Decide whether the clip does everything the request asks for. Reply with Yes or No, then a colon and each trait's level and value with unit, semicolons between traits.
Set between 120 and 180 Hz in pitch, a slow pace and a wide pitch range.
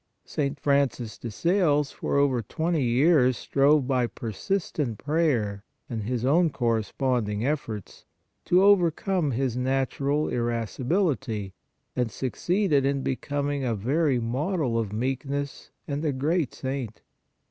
No: low, 135 Hz; slow, 125 wpm; average, 4.1 semitones